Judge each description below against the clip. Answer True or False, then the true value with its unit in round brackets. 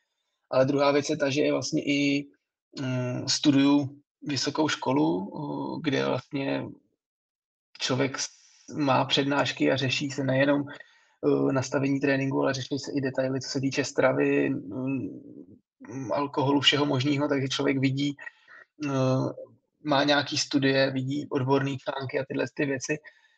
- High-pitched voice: False (140 Hz)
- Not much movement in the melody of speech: True (1.3 semitones)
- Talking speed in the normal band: True (125 wpm)